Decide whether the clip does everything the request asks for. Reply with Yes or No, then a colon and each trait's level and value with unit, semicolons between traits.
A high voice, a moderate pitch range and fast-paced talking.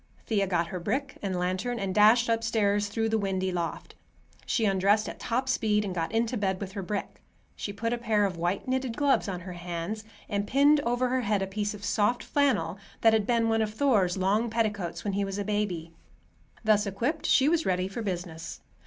Yes: high, 210 Hz; average, 3.3 semitones; fast, 210 wpm